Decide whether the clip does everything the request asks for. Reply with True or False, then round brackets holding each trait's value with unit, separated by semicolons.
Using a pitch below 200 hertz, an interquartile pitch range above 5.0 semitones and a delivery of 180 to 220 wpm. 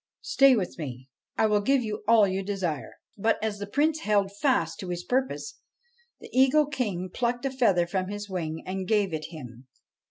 False (205 Hz; 5.6 semitones; 190 wpm)